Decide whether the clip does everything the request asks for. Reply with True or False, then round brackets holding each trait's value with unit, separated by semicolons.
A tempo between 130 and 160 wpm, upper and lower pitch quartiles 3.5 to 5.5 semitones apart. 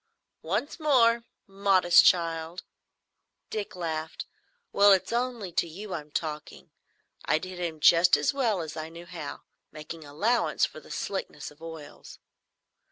True (140 wpm; 4.0 semitones)